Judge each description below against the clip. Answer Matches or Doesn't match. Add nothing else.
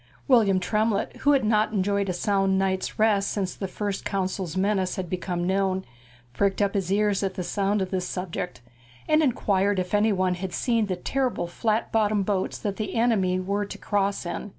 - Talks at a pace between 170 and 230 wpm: Matches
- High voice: Matches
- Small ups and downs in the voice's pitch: Matches